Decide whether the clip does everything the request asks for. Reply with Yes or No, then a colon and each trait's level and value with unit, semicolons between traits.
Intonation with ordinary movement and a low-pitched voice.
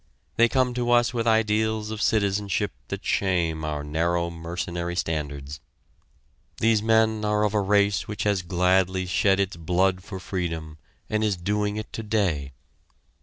Yes: average, 3.8 semitones; low, 100 Hz